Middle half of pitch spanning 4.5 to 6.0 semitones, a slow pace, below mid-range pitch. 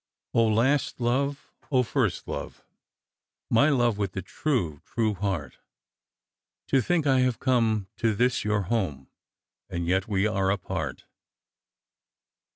Yes: average, 4.8 semitones; slow, 125 wpm; low, 110 Hz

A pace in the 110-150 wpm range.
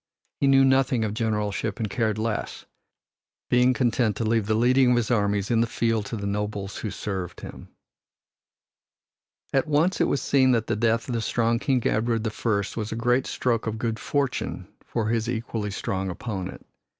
No: average, 185 wpm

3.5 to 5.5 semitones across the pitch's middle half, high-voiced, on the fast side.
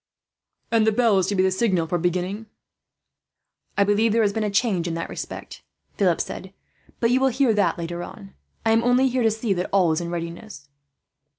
Yes: average, 4.3 semitones; high, 200 Hz; fast, 210 wpm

